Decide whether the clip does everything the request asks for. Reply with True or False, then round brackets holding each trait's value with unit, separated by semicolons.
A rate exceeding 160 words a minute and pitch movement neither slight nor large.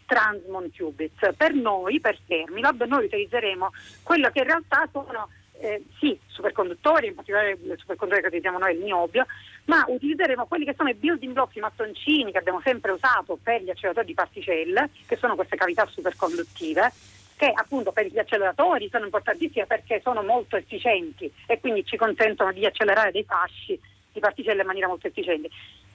False (170 wpm; 6.5 semitones)